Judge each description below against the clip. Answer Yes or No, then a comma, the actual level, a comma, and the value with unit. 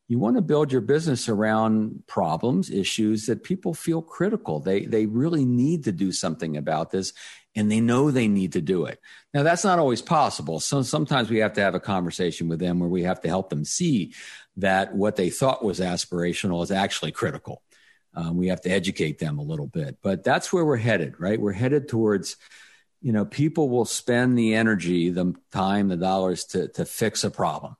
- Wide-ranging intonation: Yes, wide, 6.7 semitones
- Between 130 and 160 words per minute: No, fast, 205 wpm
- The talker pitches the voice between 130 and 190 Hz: No, low, 105 Hz